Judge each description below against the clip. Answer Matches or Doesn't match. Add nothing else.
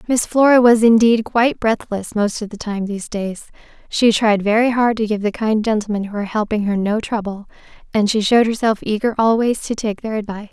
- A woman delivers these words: Matches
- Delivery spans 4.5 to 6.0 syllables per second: Matches